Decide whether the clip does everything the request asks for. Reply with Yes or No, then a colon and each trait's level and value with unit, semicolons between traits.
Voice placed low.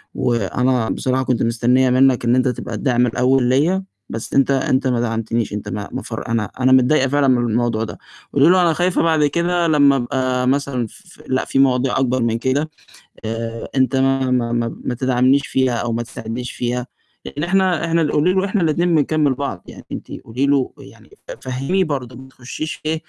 Yes: low, 130 Hz